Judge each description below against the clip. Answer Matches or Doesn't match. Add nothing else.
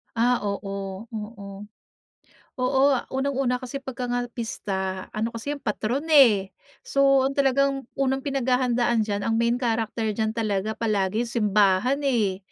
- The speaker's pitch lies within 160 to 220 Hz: Doesn't match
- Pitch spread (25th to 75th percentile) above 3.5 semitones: Matches